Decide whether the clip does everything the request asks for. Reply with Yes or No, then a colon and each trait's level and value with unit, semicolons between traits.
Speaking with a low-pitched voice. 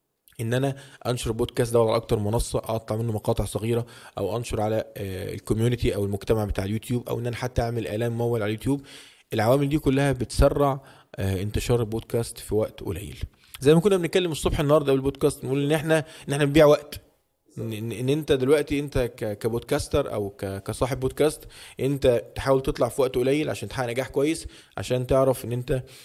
Yes: low, 125 Hz